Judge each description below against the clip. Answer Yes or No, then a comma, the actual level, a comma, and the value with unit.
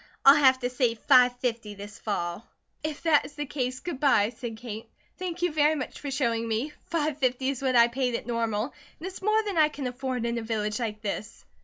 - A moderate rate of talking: No, fast, 225 wpm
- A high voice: Yes, very high, 250 Hz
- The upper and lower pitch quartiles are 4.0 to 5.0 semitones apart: Yes, average, 4.4 semitones